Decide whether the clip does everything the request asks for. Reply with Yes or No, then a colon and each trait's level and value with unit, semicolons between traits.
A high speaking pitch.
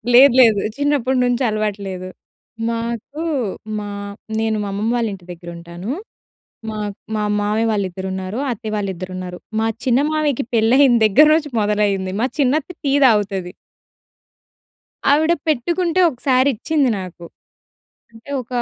Yes: high, 225 Hz